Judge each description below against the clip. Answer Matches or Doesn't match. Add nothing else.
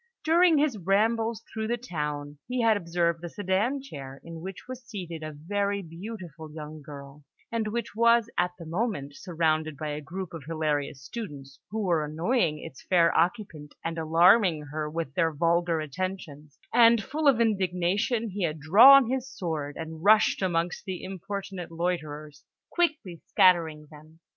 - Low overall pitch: Doesn't match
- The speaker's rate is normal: Matches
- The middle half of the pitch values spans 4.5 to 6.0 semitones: Matches